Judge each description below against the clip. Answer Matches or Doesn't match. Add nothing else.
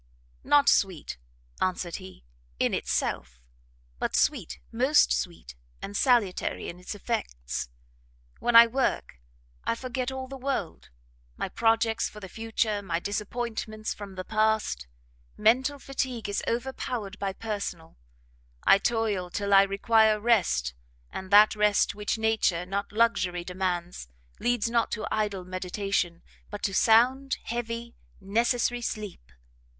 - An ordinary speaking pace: Doesn't match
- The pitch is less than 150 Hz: Doesn't match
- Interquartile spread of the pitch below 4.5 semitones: Matches